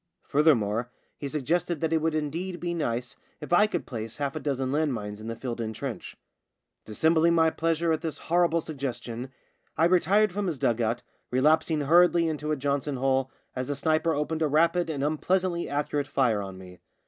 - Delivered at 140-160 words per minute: No, average, 195 wpm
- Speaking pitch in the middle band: Yes, medium, 150 Hz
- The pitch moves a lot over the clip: No, average, 4.4 semitones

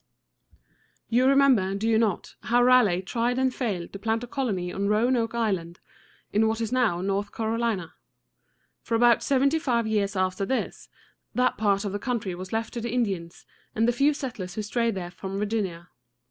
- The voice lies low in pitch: No, high, 220 Hz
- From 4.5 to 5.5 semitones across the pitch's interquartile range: No, average, 3.8 semitones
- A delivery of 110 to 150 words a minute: No, average, 180 wpm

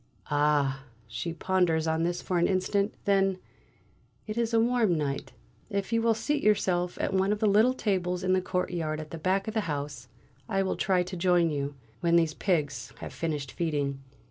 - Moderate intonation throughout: Yes, average, 4.3 semitones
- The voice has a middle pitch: Yes, medium, 180 Hz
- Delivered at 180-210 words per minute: Yes, average, 195 wpm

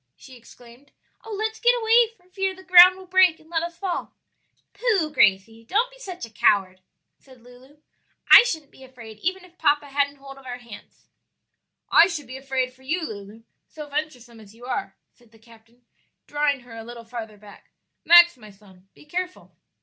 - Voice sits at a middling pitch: No, very high, 275 Hz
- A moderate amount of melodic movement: No, wide, 7.4 semitones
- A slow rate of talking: No, average, 190 wpm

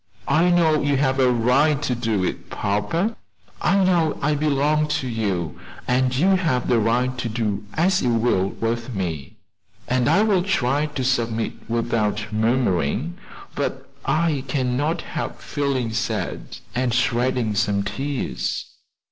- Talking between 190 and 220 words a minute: No, average, 145 wpm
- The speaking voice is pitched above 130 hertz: No, low, 125 Hz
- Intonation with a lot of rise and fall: No, average, 4.8 semitones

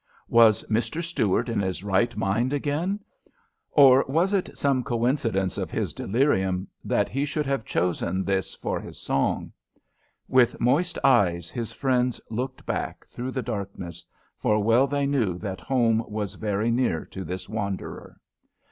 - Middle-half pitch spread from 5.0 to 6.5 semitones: Yes, wide, 5.5 semitones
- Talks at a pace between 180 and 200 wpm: No, average, 150 wpm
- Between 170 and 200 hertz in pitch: No, low, 115 Hz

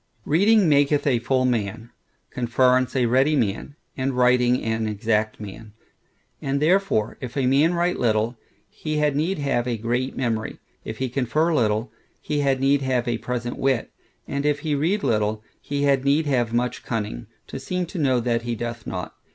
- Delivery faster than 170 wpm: Yes, average, 180 wpm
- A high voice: No, low, 130 Hz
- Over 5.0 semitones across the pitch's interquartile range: No, average, 3.5 semitones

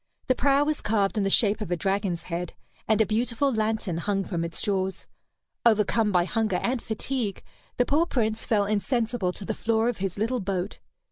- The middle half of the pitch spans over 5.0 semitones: No, average, 3.1 semitones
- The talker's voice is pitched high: Yes, high, 215 Hz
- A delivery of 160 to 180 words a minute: No, average, 195 wpm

